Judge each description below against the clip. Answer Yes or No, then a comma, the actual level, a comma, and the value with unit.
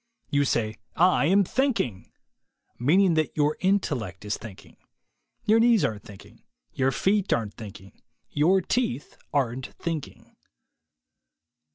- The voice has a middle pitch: Yes, medium, 145 Hz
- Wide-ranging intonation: Yes, wide, 9.0 semitones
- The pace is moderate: No, slow, 125 wpm